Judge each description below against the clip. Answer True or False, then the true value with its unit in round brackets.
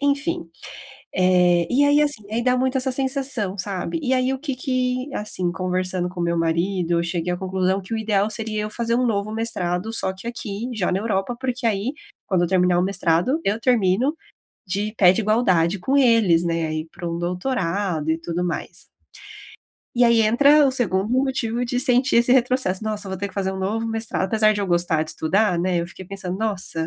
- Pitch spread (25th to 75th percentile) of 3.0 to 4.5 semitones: False (5.2 semitones)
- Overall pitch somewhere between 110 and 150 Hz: False (205 Hz)